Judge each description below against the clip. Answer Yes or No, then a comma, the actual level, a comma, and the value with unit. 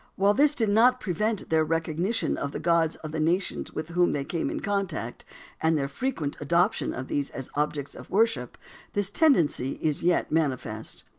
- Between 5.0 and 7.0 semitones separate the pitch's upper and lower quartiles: Yes, wide, 5.4 semitones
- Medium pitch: Yes, medium, 165 Hz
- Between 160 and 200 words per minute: Yes, average, 180 wpm